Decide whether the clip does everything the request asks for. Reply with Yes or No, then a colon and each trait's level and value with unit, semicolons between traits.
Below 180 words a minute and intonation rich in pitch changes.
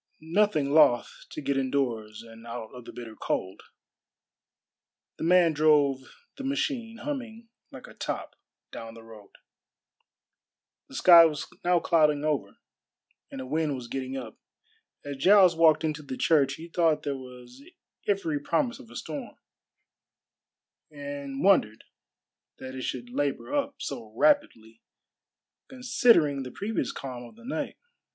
Yes: average, 140 wpm; wide, 6.0 semitones